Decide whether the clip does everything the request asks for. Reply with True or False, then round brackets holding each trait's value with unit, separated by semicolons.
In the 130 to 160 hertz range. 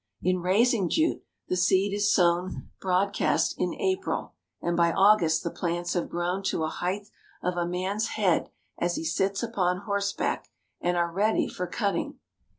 False (185 Hz)